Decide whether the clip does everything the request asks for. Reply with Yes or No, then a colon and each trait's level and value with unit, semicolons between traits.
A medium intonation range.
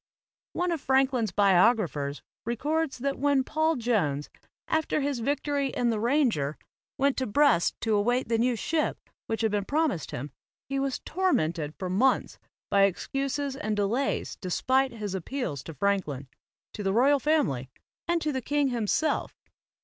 No: wide, 6.0 semitones